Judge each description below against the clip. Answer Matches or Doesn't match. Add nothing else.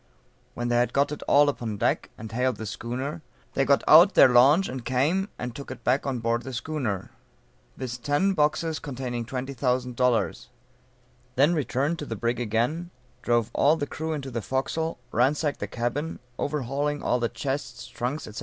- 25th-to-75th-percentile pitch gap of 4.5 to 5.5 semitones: Doesn't match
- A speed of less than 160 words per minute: Doesn't match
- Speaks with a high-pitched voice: Doesn't match